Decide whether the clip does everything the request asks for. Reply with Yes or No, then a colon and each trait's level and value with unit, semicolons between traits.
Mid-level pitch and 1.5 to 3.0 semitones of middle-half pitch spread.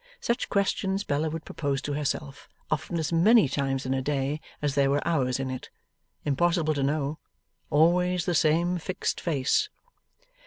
No: medium, 150 Hz; average, 3.8 semitones